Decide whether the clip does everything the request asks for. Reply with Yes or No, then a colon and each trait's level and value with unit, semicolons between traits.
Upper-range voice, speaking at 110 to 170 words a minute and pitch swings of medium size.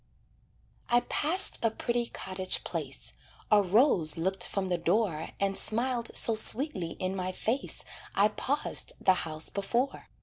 Yes: high, 200 Hz; average, 140 wpm; average, 4.4 semitones